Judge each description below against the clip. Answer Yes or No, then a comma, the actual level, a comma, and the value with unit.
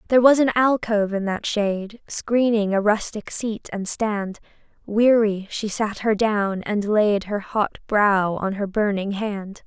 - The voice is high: Yes, high, 210 Hz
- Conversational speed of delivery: Yes, average, 170 wpm